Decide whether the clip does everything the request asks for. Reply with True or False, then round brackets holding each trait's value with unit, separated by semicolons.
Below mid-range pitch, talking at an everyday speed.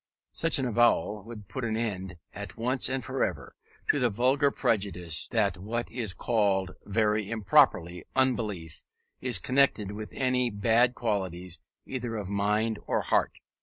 True (110 Hz; 150 wpm)